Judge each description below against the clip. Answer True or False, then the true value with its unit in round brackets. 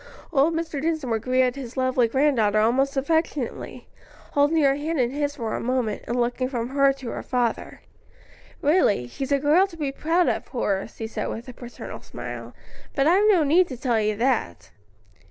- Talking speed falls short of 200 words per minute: True (185 wpm)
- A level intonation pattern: False (3.9 semitones)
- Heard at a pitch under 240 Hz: False (270 Hz)